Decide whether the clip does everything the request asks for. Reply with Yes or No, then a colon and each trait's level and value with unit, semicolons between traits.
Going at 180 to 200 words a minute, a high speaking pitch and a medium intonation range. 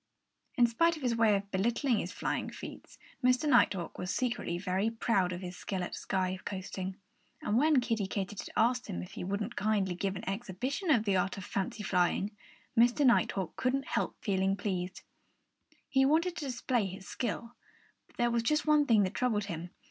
Yes: average, 185 wpm; high, 210 Hz; average, 4.5 semitones